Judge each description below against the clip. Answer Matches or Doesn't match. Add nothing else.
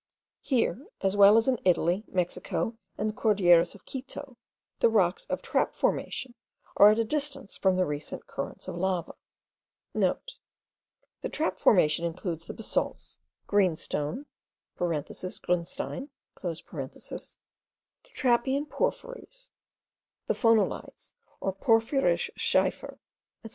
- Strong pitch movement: Matches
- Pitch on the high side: Matches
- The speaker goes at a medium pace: Doesn't match